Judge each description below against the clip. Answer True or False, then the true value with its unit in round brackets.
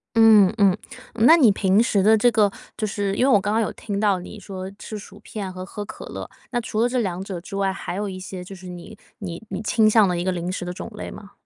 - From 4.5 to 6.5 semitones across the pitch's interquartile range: False (2.5 semitones)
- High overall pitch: True (200 Hz)